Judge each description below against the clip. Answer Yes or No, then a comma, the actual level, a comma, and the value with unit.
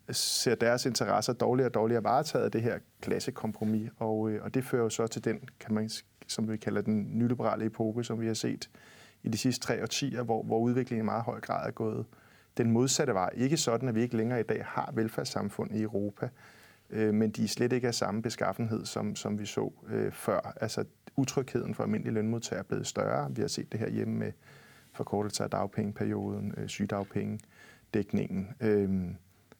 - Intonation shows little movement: Yes, narrow, 2.1 semitones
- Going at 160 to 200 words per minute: Yes, average, 195 wpm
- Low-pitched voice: Yes, low, 110 Hz